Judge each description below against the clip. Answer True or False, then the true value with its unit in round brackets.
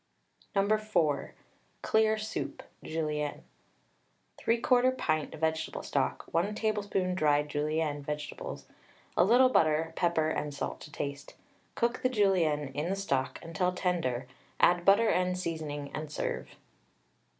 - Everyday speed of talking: False (125 wpm)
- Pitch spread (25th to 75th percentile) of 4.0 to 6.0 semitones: True (4.9 semitones)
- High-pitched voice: False (165 Hz)